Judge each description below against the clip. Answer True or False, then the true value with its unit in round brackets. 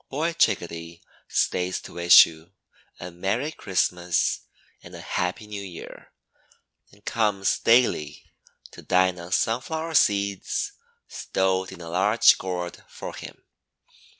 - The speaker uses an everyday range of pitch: True (3.4 semitones)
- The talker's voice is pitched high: False (95 Hz)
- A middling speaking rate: False (125 wpm)